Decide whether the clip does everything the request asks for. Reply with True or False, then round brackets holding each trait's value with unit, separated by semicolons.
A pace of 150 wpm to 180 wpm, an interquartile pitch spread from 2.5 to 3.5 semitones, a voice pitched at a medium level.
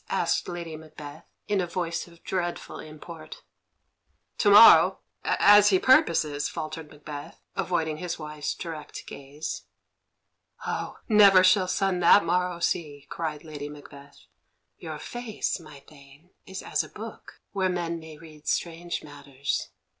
False (135 wpm; 3.1 semitones; 165 Hz)